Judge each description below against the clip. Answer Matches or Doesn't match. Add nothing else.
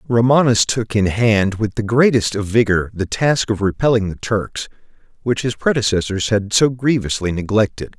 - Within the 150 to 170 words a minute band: Matches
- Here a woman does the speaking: Doesn't match